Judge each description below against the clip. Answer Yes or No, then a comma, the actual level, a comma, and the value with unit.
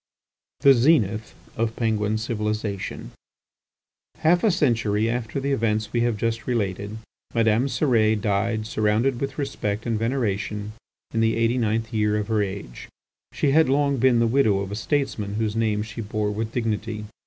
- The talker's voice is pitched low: Yes, low, 110 Hz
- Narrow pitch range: Yes, narrow, 2.2 semitones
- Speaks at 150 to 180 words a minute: Yes, average, 160 wpm